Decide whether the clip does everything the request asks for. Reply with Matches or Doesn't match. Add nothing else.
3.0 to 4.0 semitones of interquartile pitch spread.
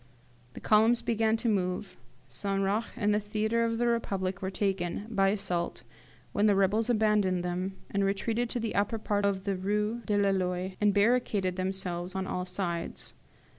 Doesn't match